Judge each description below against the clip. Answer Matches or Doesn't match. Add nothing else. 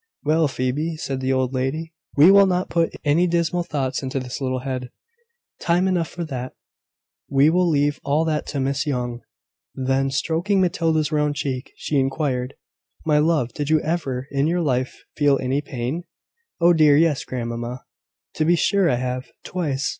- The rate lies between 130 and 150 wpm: Doesn't match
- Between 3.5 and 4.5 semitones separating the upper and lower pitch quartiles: Matches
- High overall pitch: Doesn't match